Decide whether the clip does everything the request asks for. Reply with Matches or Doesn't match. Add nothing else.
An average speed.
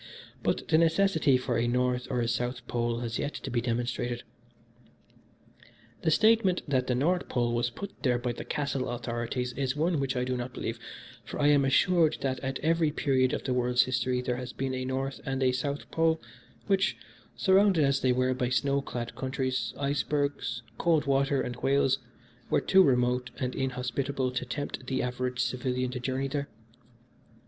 Matches